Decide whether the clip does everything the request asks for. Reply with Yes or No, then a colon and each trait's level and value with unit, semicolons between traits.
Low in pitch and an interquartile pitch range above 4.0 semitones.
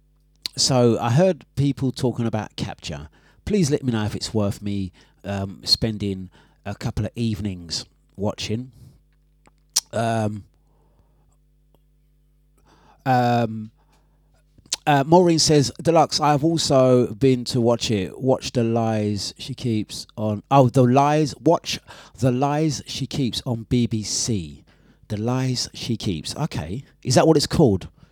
Yes: low, 125 Hz; wide, 5.4 semitones